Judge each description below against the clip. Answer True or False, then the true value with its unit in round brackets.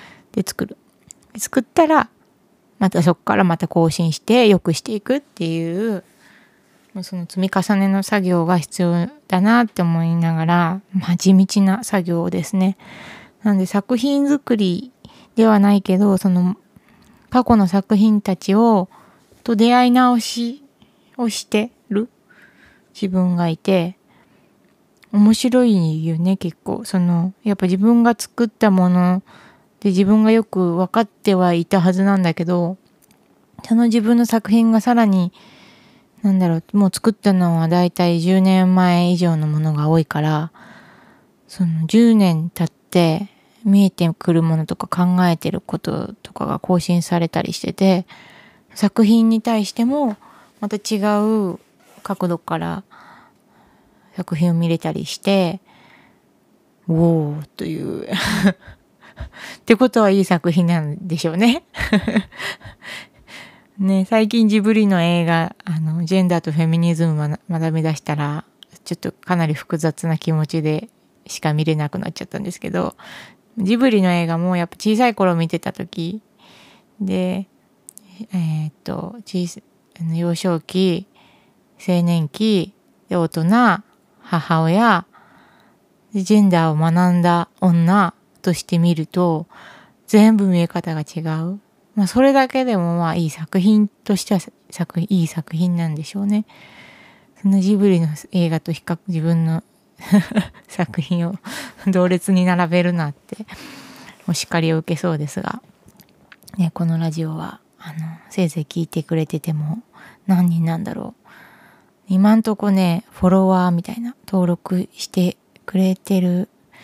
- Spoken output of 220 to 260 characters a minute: True (255 characters per minute)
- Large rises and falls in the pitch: False (3.8 semitones)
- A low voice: False (185 Hz)